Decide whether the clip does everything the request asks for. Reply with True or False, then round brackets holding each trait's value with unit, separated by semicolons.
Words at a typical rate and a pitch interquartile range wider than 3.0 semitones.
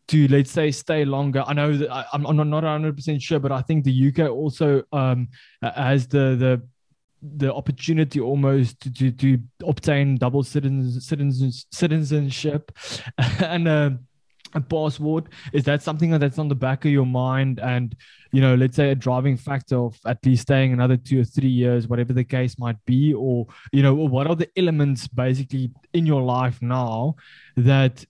False (175 wpm; 2.7 semitones)